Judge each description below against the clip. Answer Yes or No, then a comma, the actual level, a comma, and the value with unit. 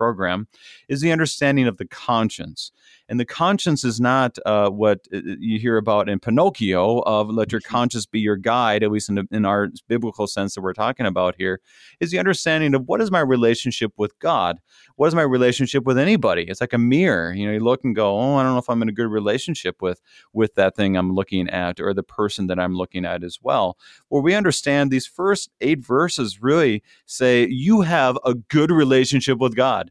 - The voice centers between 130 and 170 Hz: No, low, 120 Hz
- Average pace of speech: No, fast, 215 wpm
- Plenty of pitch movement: No, average, 4.5 semitones